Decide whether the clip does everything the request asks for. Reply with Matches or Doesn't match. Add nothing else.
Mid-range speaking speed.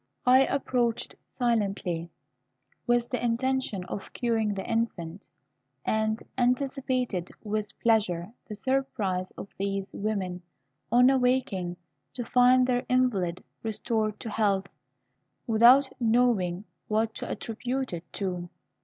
Doesn't match